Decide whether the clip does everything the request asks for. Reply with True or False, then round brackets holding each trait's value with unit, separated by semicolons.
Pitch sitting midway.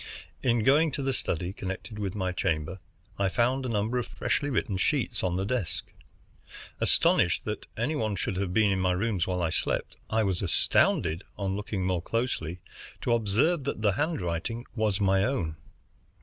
False (100 Hz)